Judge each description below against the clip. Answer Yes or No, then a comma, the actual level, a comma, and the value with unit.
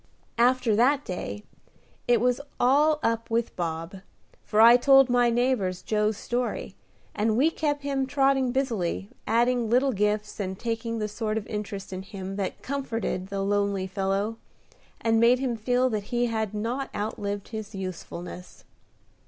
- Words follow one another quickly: No, average, 155 wpm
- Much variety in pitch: No, average, 3.7 semitones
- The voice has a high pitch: Yes, high, 225 Hz